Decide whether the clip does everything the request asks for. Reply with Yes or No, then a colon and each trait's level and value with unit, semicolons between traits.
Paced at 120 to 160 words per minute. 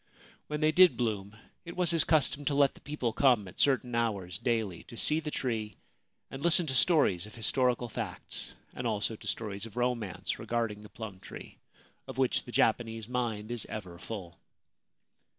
No: average, 180 wpm